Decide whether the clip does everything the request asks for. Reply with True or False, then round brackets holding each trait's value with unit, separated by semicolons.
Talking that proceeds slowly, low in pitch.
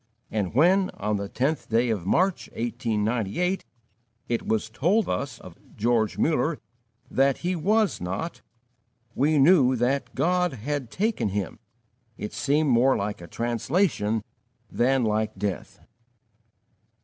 True (125 wpm; 125 Hz)